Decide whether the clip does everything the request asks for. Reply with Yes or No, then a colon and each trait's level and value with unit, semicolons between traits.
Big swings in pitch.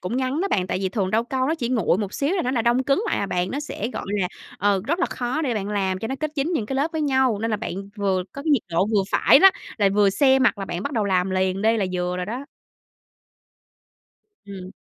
Yes: wide, 5.7 semitones